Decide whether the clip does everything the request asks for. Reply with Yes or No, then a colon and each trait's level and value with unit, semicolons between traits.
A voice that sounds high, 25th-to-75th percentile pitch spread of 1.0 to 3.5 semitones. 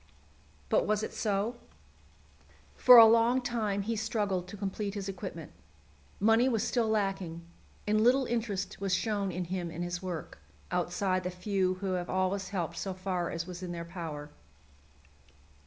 Yes: high, 195 Hz; average, 3.1 semitones